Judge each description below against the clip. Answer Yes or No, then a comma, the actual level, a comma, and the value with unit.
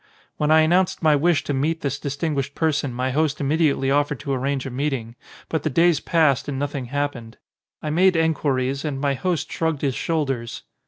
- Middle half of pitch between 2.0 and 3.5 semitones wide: Yes, average, 2.8 semitones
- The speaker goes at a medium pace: Yes, average, 195 wpm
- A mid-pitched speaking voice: Yes, medium, 145 Hz